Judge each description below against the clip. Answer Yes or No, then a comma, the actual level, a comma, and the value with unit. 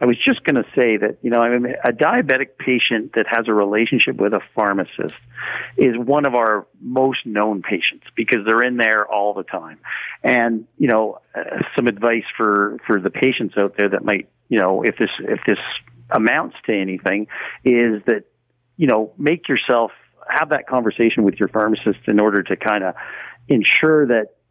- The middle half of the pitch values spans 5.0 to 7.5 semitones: No, average, 2.8 semitones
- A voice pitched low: Yes, low, 110 Hz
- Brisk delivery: No, average, 190 wpm